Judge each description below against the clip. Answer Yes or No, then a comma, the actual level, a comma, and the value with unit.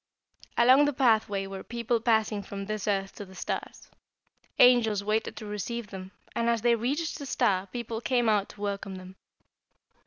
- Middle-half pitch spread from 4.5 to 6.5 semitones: No, average, 3.1 semitones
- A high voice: Yes, high, 215 Hz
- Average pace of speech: Yes, average, 175 wpm